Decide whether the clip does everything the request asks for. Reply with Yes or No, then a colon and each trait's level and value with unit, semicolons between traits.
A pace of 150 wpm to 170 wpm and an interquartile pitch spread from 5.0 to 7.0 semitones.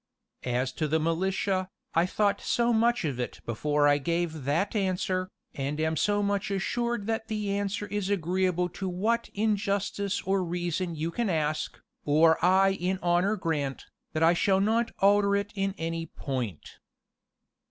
No: average, 165 wpm; average, 3.9 semitones